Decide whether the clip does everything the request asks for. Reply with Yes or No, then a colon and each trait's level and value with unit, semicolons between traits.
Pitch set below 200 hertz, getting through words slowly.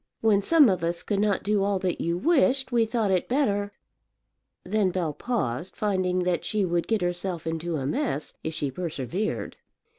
No: medium, 185 Hz; average, 185 wpm